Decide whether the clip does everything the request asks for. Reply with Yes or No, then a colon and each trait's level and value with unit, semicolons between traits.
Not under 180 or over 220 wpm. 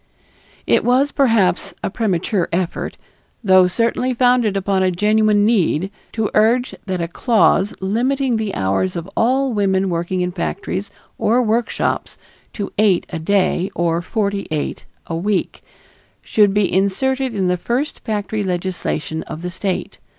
No: average, 145 wpm